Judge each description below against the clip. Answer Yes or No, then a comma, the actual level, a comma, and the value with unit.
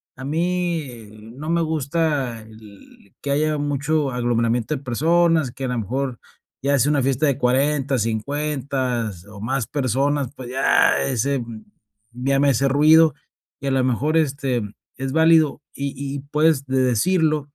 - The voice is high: No, low, 135 Hz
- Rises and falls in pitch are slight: No, average, 3.3 semitones